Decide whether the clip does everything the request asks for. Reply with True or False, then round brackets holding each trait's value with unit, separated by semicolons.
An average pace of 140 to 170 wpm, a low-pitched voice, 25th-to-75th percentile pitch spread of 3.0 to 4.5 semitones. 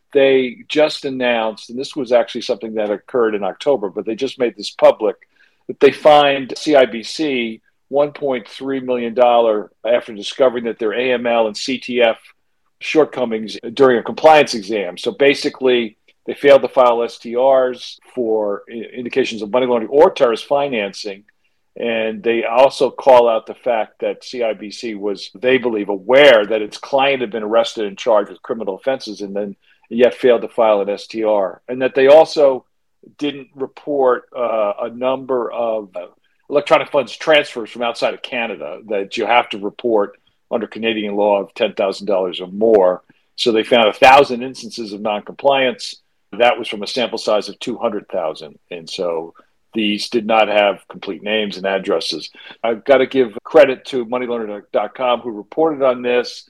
True (155 wpm; 120 Hz; 3.5 semitones)